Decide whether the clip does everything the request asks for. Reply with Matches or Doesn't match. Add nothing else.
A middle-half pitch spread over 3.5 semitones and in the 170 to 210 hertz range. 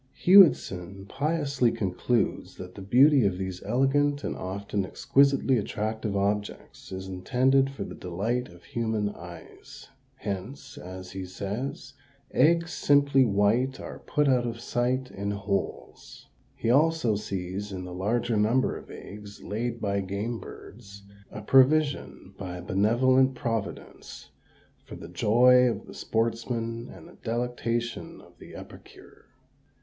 Doesn't match